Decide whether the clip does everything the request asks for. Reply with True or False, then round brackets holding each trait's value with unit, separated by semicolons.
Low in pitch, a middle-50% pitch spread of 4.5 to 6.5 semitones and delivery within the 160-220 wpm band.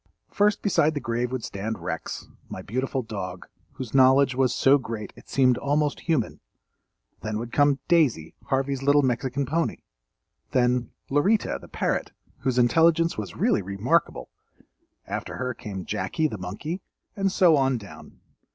False (130 Hz; 4.8 semitones; 150 wpm)